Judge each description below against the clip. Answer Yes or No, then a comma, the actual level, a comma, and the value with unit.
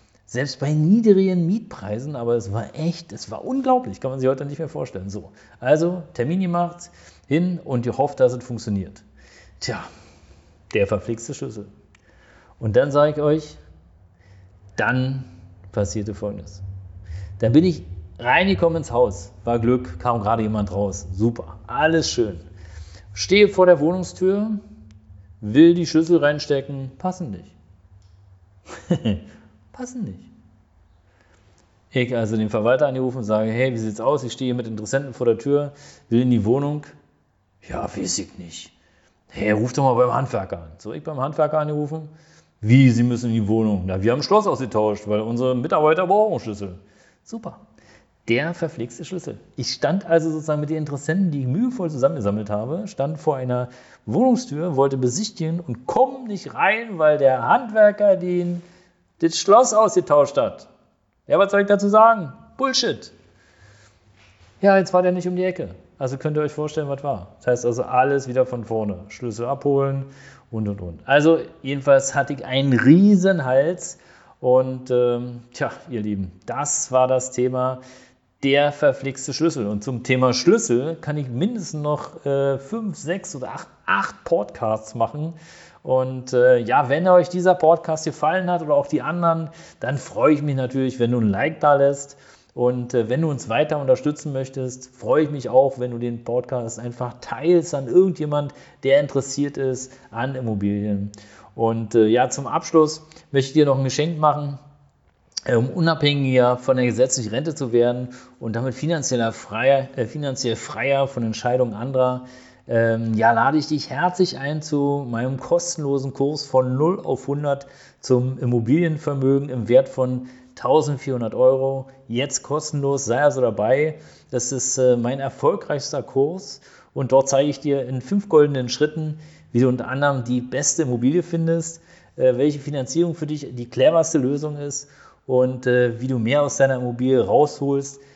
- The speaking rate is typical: Yes, average, 160 wpm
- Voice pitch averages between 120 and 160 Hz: Yes, low, 135 Hz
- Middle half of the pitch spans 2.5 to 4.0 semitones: No, average, 4.7 semitones